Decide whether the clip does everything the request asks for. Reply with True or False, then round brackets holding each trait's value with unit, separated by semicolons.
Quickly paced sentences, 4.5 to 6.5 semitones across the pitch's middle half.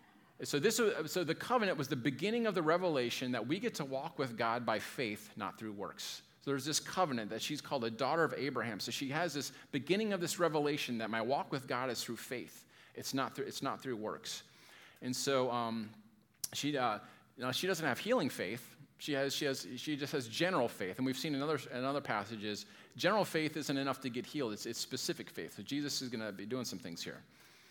True (235 wpm; 5.0 semitones)